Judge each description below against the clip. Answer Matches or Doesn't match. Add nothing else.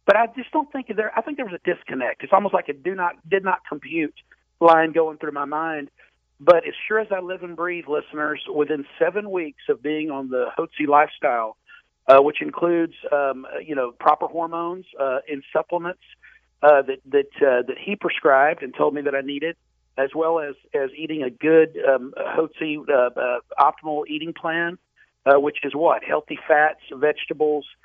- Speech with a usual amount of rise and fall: Matches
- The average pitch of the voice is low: Doesn't match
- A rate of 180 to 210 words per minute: Matches